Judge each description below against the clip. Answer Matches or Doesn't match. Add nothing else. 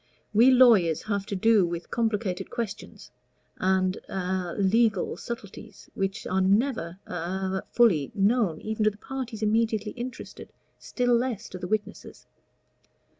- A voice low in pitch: Doesn't match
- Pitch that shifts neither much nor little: Matches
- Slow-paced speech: Matches